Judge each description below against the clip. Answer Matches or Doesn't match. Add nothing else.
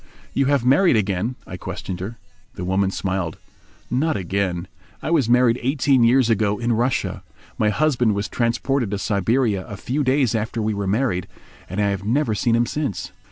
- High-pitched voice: Doesn't match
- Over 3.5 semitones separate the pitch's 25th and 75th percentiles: Matches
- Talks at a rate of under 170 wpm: Doesn't match